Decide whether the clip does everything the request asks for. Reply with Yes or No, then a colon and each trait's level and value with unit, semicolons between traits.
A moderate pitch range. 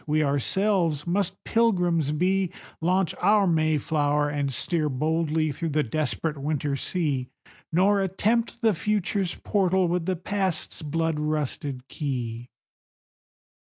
Yes: average, 4.3 semitones